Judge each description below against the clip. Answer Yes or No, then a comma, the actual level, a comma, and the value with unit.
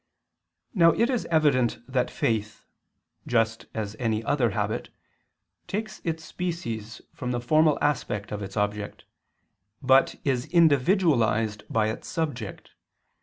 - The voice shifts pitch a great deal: Yes, wide, 6.2 semitones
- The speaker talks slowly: Yes, slow, 120 wpm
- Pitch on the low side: Yes, low, 125 Hz